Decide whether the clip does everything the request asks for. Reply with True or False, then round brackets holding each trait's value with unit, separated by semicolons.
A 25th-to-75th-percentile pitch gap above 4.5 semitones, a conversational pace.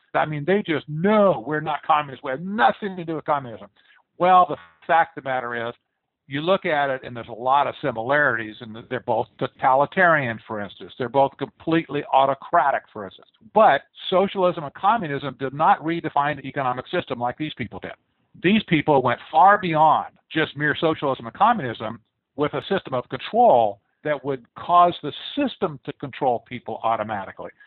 True (4.9 semitones; 180 wpm)